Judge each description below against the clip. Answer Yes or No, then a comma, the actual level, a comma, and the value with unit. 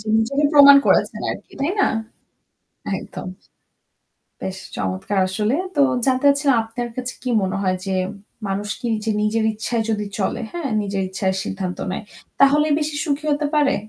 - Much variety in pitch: Yes, wide, 6.3 semitones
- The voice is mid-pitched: No, high, 225 Hz